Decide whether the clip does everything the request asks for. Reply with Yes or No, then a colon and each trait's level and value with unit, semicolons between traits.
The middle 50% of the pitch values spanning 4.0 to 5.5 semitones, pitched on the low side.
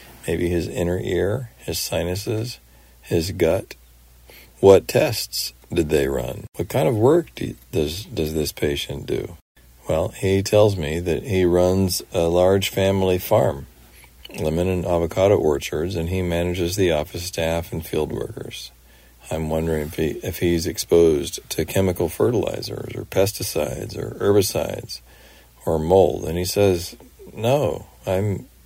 No: average, 3.5 semitones; very low, 85 Hz